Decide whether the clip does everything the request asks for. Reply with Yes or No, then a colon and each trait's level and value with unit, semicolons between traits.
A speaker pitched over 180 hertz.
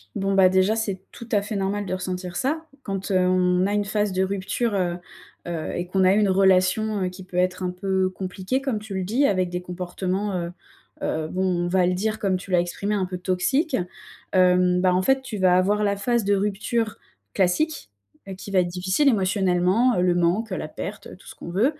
Yes: high, 190 Hz